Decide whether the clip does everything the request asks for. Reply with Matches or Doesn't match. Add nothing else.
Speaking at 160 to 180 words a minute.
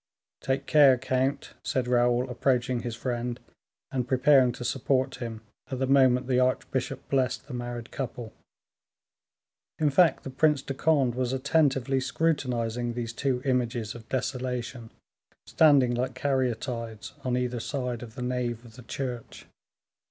Doesn't match